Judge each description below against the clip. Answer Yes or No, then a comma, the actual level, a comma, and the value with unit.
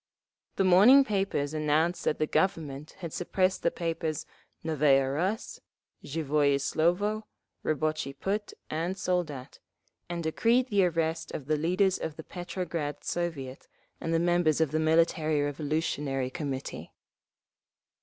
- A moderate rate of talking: No, slow, 125 wpm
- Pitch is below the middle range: No, medium, 160 Hz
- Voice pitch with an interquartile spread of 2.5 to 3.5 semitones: Yes, average, 3.2 semitones